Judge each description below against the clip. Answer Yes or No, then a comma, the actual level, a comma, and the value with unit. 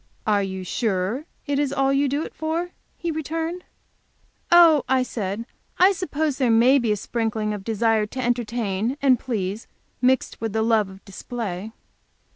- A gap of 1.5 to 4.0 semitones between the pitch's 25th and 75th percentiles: No, average, 5.0 semitones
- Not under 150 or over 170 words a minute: Yes, average, 165 wpm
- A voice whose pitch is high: Yes, high, 240 Hz